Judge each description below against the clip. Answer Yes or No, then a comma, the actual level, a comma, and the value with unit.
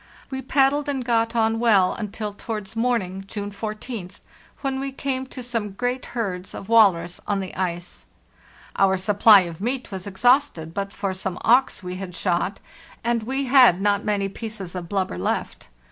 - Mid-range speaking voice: No, high, 210 Hz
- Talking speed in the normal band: Yes, average, 175 wpm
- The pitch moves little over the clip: No, average, 4.3 semitones